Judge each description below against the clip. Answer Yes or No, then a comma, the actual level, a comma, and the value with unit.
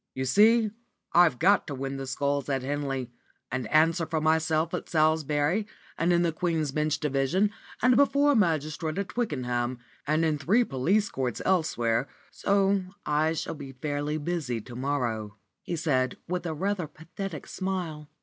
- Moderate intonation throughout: Yes, average, 4.5 semitones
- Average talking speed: Yes, average, 160 wpm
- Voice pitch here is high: No, medium, 155 Hz